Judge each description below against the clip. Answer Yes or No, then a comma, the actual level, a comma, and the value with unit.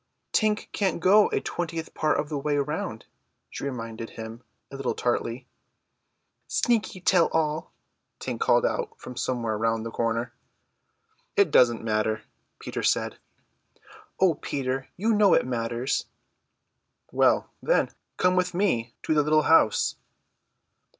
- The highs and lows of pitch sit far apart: Yes, wide, 7.6 semitones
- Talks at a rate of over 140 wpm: No, slow, 135 wpm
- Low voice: No, medium, 145 Hz